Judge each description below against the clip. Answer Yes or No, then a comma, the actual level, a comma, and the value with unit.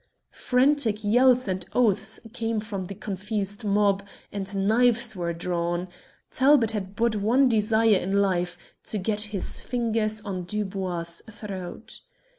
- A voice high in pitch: Yes, high, 210 Hz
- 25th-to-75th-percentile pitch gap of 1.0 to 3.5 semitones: Yes, average, 3.0 semitones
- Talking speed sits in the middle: No, slow, 130 wpm